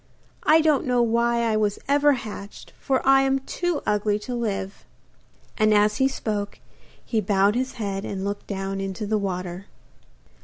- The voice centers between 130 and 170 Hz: No, high, 215 Hz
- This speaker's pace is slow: No, average, 165 wpm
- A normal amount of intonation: Yes, average, 4.4 semitones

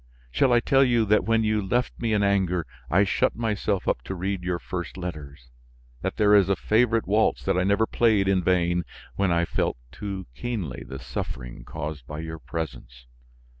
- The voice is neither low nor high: No, very low, 95 Hz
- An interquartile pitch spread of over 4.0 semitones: Yes, average, 4.6 semitones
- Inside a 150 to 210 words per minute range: Yes, average, 190 wpm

